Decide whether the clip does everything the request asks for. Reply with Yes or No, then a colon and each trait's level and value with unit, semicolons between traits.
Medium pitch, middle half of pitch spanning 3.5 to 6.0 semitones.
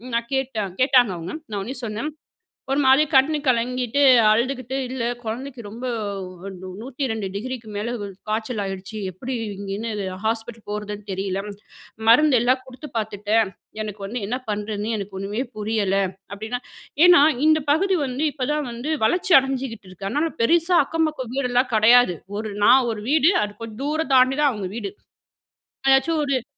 No: high, 235 Hz; average, 4.2 semitones